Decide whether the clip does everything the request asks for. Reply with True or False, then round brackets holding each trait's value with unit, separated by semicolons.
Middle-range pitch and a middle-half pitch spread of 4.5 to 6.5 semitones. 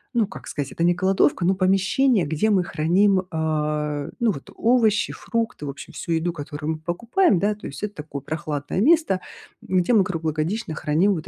True (175 Hz; 5.2 semitones)